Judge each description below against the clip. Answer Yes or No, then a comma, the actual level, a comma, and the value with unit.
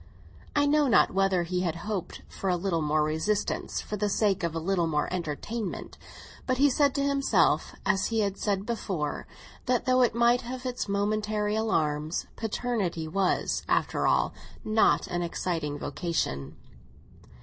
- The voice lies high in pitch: Yes, high, 195 Hz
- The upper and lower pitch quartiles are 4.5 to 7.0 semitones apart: Yes, wide, 5.4 semitones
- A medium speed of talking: Yes, average, 160 wpm